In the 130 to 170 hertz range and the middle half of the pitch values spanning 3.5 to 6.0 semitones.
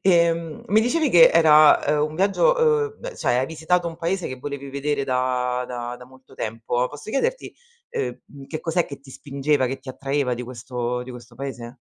Yes: medium, 140 Hz; average, 5.0 semitones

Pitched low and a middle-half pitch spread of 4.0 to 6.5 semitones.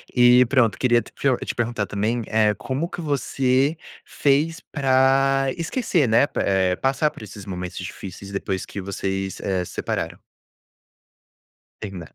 Yes: low, 120 Hz; wide, 5.5 semitones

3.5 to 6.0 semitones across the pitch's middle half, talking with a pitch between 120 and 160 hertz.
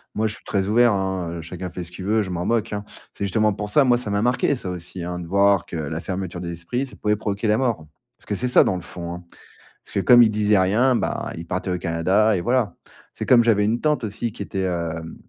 No: average, 3.8 semitones; low, 100 Hz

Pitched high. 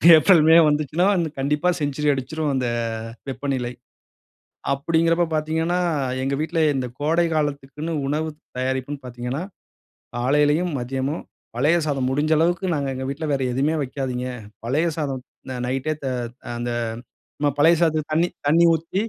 No: medium, 150 Hz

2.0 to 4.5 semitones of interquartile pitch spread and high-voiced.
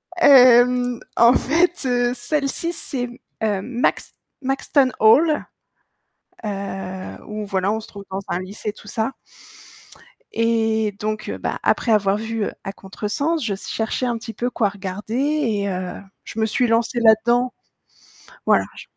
Yes: average, 3.4 semitones; high, 225 Hz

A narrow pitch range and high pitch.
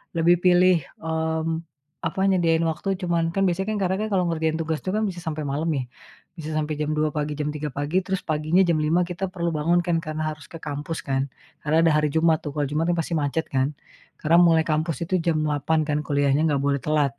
No: narrow, 2.3 semitones; medium, 160 Hz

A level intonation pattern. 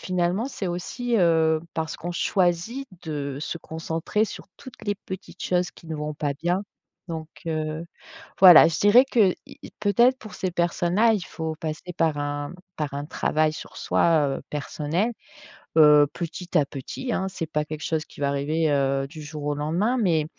No: average, 3.5 semitones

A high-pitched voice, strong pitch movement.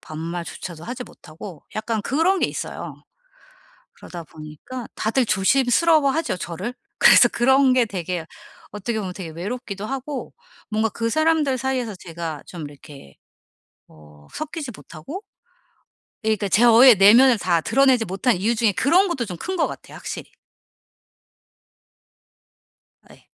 Yes: high, 220 Hz; wide, 7.0 semitones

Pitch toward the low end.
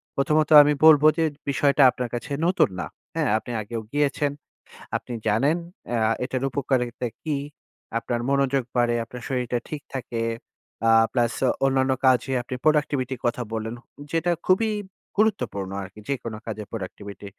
Yes: low, 125 Hz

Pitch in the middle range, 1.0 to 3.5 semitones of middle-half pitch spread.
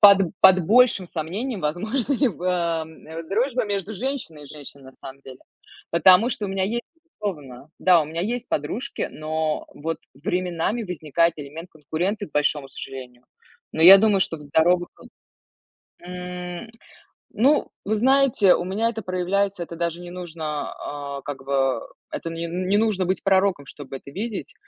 No: medium, 180 Hz; average, 4.7 semitones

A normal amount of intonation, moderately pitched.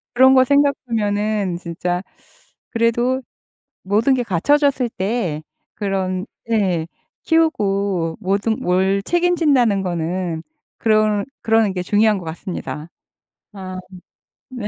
No: average, 4.7 semitones; high, 205 Hz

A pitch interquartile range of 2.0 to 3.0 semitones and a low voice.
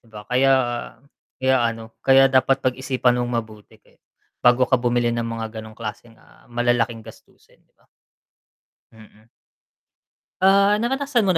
Yes: narrow, 2.6 semitones; low, 120 Hz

